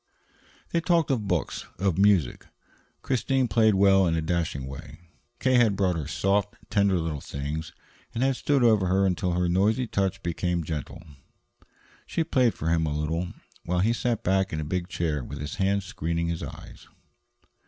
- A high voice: No, very low, 95 Hz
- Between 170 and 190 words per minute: Yes, average, 175 wpm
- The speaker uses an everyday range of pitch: Yes, average, 4.2 semitones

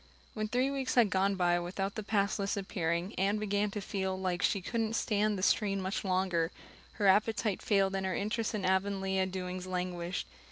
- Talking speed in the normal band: Yes, average, 195 wpm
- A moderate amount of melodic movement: No, narrow, 2.2 semitones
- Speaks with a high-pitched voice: Yes, high, 195 Hz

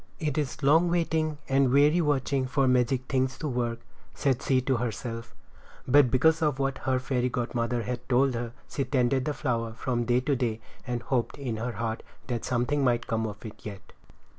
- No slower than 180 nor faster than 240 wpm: Yes, average, 190 wpm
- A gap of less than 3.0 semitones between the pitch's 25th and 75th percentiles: Yes, narrow, 2.6 semitones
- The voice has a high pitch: No, low, 130 Hz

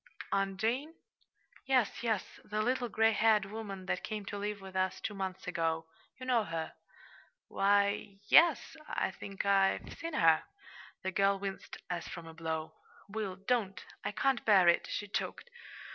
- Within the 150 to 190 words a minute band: Yes, average, 165 wpm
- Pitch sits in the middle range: No, high, 200 Hz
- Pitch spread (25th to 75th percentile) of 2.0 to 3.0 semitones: Yes, average, 2.7 semitones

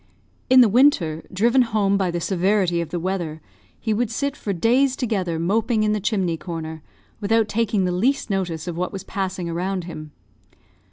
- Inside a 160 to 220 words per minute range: Yes, average, 180 wpm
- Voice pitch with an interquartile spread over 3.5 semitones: Yes, average, 4.5 semitones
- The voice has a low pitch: No, high, 195 Hz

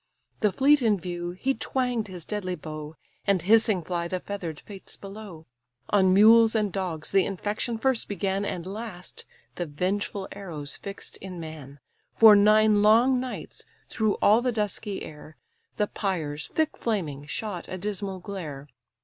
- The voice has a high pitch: Yes, high, 195 Hz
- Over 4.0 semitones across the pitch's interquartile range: No, average, 3.7 semitones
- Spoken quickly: No, average, 155 wpm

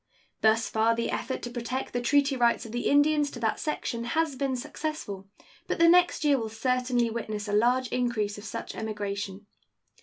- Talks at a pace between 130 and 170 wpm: No, average, 185 wpm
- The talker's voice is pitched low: No, high, 240 Hz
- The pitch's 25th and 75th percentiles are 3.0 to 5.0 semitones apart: Yes, average, 4.1 semitones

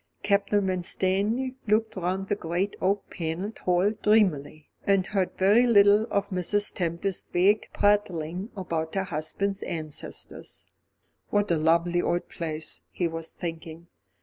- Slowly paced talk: Yes, slow, 130 wpm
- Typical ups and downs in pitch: Yes, average, 3.4 semitones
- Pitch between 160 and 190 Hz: Yes, medium, 185 Hz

